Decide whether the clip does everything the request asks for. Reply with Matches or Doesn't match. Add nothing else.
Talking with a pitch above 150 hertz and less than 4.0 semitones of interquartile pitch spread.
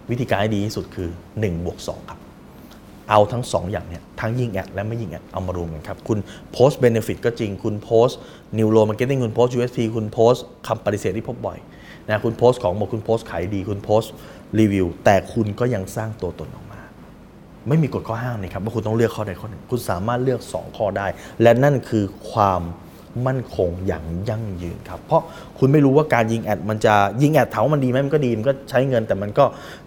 Doesn't match